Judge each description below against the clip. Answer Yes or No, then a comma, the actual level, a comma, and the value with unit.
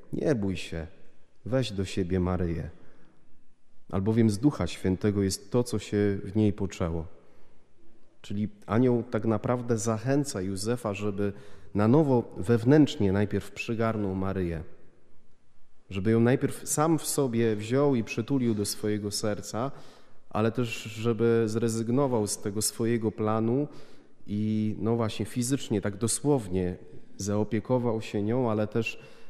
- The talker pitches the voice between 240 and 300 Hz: No, low, 110 Hz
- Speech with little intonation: No, average, 3.0 semitones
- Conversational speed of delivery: Yes, average, 125 wpm